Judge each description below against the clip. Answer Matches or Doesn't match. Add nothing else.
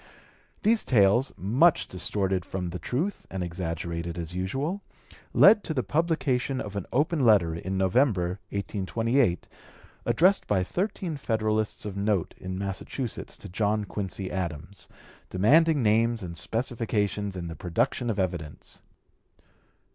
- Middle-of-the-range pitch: Doesn't match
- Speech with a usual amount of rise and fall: Doesn't match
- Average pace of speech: Doesn't match